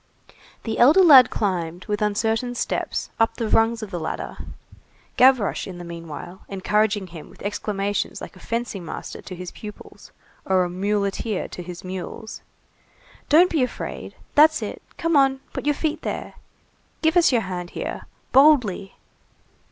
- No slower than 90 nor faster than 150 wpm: Yes, average, 140 wpm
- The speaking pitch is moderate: No, high, 210 Hz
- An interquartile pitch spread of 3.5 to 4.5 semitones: No, wide, 5.6 semitones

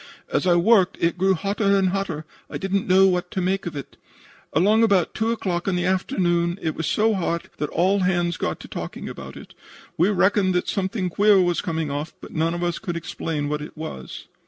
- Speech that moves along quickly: Yes, fast, 215 wpm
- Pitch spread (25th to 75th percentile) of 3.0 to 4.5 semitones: No, narrow, 2.5 semitones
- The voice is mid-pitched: Yes, medium, 180 Hz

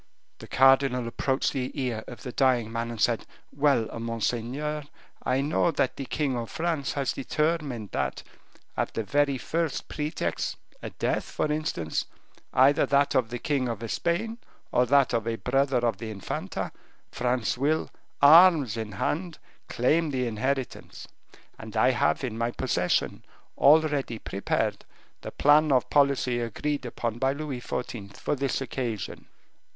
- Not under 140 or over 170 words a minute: Yes, average, 150 wpm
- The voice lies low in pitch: Yes, low, 130 Hz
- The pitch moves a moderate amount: Yes, average, 3.7 semitones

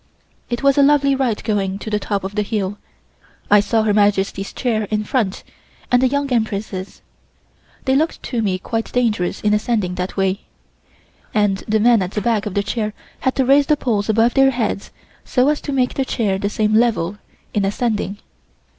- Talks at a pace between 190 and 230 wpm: Yes, average, 195 wpm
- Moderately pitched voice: No, high, 215 Hz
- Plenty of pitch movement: No, average, 3.5 semitones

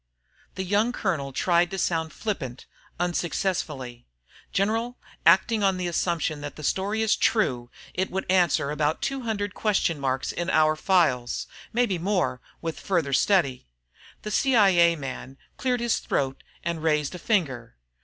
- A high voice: No, medium, 175 Hz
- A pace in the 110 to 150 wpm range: Yes, average, 145 wpm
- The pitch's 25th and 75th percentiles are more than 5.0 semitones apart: Yes, wide, 5.4 semitones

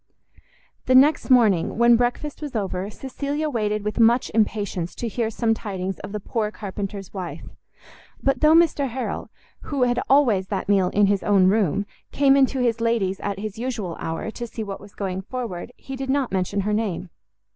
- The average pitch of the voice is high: Yes, high, 220 Hz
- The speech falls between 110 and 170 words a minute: No, average, 185 wpm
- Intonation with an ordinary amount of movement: Yes, average, 4.3 semitones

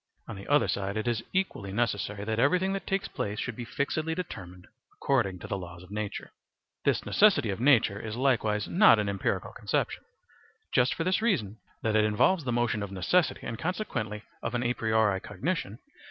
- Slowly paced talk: No, average, 185 wpm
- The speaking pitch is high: No, low, 110 Hz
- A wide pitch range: Yes, wide, 6.0 semitones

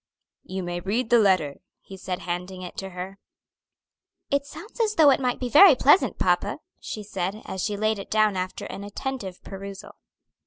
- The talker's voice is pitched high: Yes, high, 200 Hz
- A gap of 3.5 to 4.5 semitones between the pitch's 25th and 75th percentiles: No, average, 4.9 semitones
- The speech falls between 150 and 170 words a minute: No, average, 185 wpm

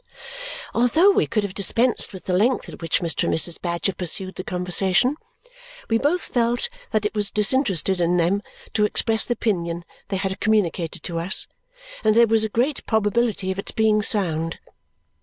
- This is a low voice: No, high, 205 Hz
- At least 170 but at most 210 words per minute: Yes, average, 180 wpm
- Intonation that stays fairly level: No, average, 4.0 semitones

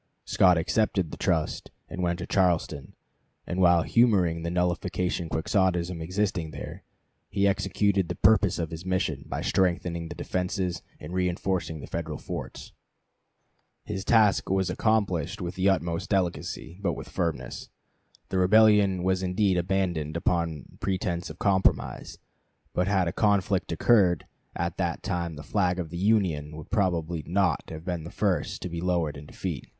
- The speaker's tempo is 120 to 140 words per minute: No, average, 155 wpm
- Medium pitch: No, very low, 90 Hz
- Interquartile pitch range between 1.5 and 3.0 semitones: Yes, narrow, 2.4 semitones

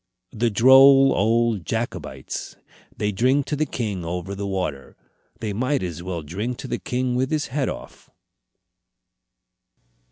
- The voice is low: Yes, low, 110 Hz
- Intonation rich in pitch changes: Yes, wide, 5.8 semitones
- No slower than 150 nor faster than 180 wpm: No, average, 140 wpm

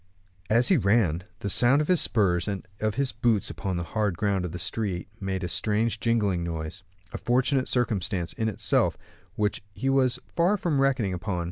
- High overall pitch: No, low, 105 Hz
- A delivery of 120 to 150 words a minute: No, average, 190 wpm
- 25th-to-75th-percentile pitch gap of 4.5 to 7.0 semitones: Yes, average, 4.9 semitones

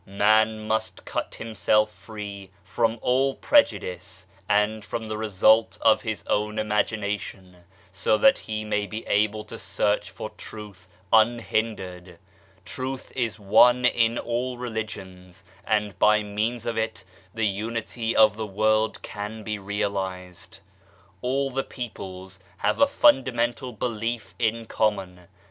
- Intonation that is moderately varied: No, narrow, 2.2 semitones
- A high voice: No, low, 110 Hz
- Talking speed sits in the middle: No, slow, 130 wpm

